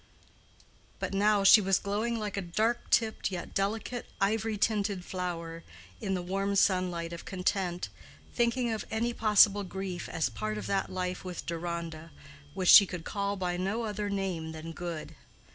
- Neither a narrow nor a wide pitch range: Yes, average, 3.0 semitones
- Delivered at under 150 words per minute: No, average, 160 wpm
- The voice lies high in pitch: Yes, high, 195 Hz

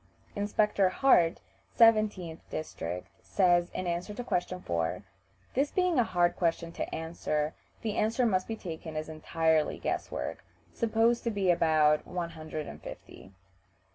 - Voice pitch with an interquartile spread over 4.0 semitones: Yes, average, 5.1 semitones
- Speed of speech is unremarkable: Yes, average, 145 wpm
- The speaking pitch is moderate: Yes, medium, 175 Hz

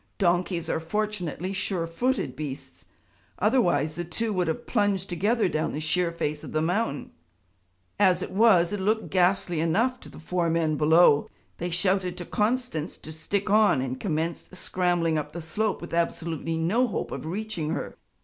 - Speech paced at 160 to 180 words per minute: Yes, average, 170 wpm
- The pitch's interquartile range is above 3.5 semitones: Yes, average, 4.1 semitones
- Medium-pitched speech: Yes, medium, 175 Hz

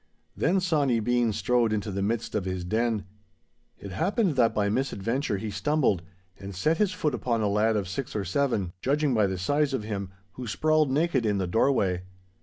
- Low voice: Yes, low, 115 Hz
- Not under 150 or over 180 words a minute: No, average, 195 wpm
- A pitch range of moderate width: No, wide, 5.7 semitones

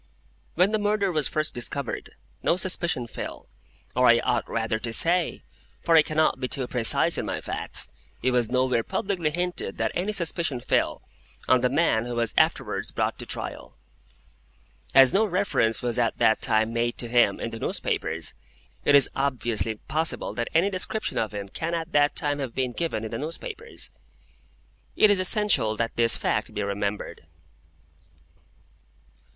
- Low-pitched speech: Yes, low, 130 Hz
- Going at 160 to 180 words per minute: Yes, average, 165 wpm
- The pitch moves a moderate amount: No, wide, 6.6 semitones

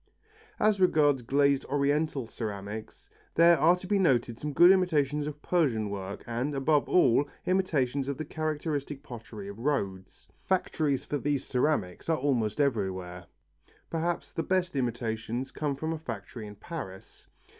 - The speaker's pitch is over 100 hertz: Yes, medium, 140 Hz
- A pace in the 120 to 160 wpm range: Yes, average, 145 wpm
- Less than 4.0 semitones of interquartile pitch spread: No, wide, 5.5 semitones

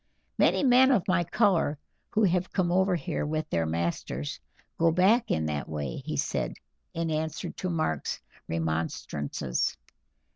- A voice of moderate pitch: Yes, medium, 160 Hz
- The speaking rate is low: No, average, 145 wpm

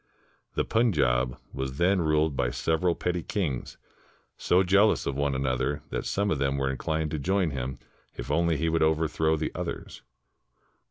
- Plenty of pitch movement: No, average, 4.3 semitones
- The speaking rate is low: No, average, 165 wpm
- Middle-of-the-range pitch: No, very low, 80 Hz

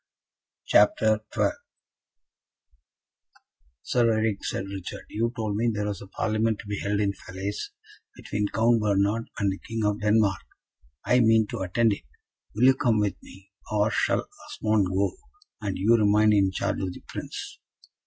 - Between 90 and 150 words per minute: No, average, 160 wpm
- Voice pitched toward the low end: Yes, low, 105 Hz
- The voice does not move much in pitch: Yes, narrow, 1.9 semitones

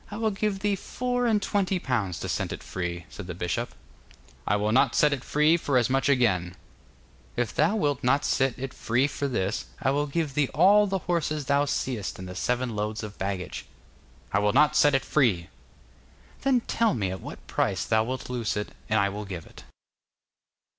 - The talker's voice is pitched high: No, low, 130 Hz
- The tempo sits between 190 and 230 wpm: Yes, average, 200 wpm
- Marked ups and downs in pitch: Yes, wide, 6.7 semitones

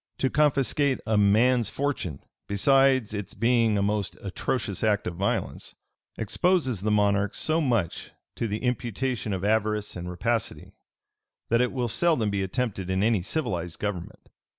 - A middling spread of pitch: Yes, average, 4.1 semitones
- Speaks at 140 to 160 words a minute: Yes, average, 150 wpm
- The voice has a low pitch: Yes, low, 110 Hz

